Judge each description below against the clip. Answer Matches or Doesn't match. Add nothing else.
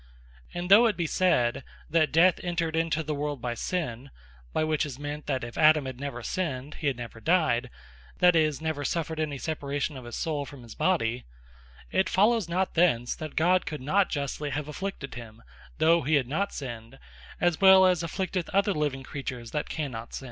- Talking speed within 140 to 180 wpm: Doesn't match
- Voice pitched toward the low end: Doesn't match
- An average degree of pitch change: Matches